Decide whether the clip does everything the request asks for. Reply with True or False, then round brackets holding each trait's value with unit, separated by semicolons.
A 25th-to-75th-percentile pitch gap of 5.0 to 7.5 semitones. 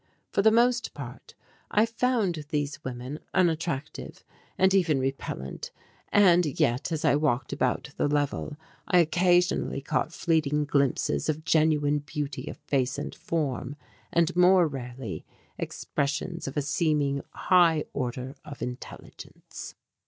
False (4.1 semitones)